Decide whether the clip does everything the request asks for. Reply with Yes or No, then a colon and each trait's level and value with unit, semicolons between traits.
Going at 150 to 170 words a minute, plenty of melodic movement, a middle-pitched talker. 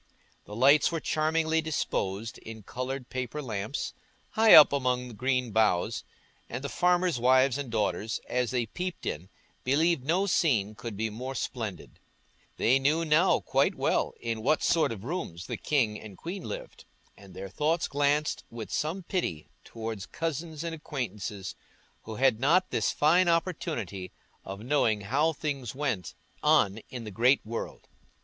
No: average, 155 wpm; wide, 5.9 semitones; low, 130 Hz